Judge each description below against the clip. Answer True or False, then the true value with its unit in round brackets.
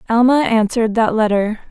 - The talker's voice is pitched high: True (225 Hz)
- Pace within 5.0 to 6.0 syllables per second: True (5.6 syllables/s)